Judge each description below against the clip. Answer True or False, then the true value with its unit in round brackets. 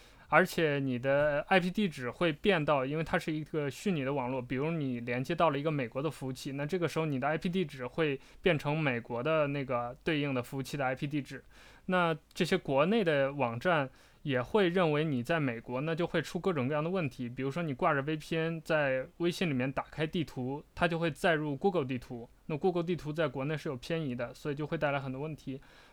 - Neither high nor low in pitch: True (150 Hz)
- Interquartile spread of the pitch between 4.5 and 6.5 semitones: False (4.0 semitones)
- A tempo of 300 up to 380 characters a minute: True (350 characters per minute)